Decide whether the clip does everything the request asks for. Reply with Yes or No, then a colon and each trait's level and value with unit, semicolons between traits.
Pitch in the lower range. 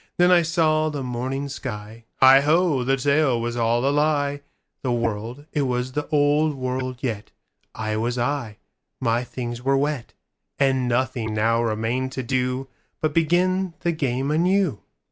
Yes: low, 130 Hz